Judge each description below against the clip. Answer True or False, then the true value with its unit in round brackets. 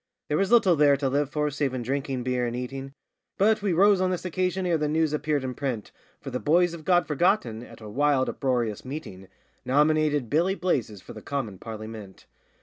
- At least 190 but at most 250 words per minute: True (205 wpm)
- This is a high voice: False (145 Hz)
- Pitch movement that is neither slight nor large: True (4.8 semitones)